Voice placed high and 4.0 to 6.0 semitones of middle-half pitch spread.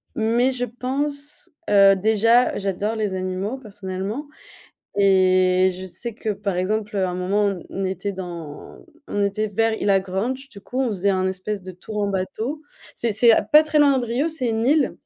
Yes: high, 205 Hz; average, 4.4 semitones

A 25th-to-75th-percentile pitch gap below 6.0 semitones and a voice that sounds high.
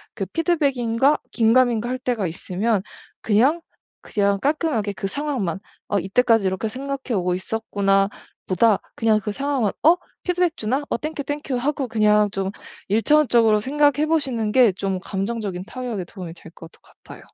Yes: wide, 5.6 semitones; high, 225 Hz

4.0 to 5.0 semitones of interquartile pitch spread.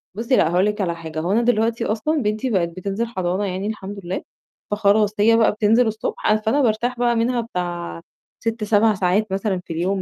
No: average, 3.4 semitones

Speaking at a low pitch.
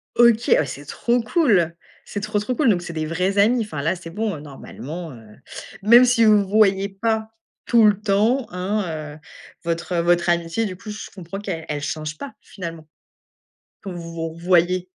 No: high, 190 Hz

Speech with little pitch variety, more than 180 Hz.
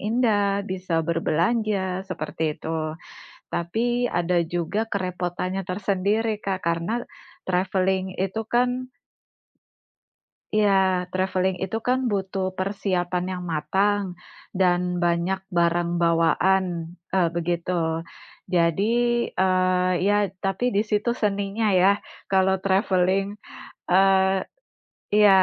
Yes: narrow, 2.2 semitones; high, 190 Hz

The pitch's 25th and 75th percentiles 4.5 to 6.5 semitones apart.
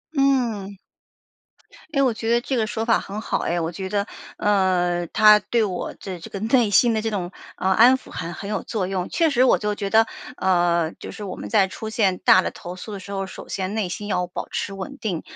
No: average, 3.3 semitones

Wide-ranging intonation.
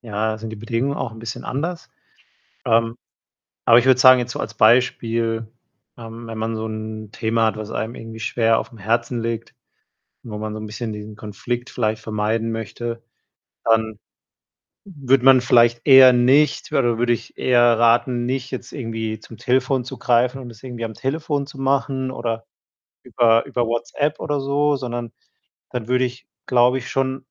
No: narrow, 2.4 semitones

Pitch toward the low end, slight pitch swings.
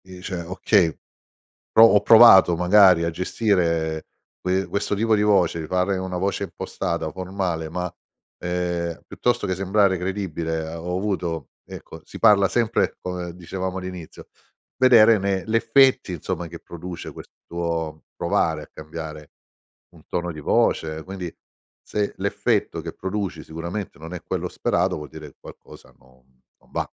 No: very low, 90 Hz; average, 3.0 semitones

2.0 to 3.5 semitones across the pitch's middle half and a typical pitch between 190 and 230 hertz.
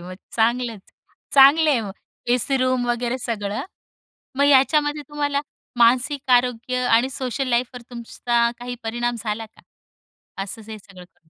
No: narrow, 2.6 semitones; high, 245 Hz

